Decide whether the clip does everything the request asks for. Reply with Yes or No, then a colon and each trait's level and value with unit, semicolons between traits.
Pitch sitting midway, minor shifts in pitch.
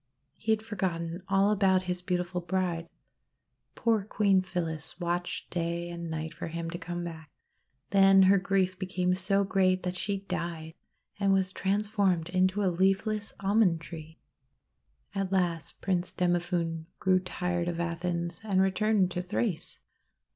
Yes: medium, 180 Hz; narrow, 2.2 semitones